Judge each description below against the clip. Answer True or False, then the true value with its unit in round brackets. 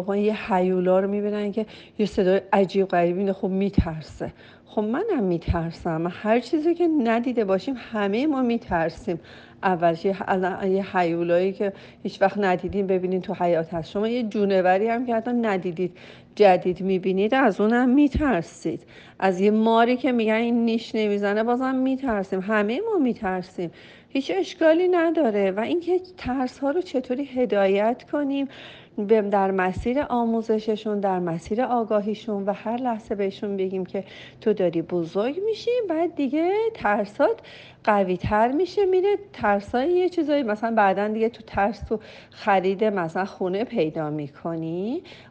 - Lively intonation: False (4.5 semitones)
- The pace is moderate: True (145 wpm)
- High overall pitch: True (210 Hz)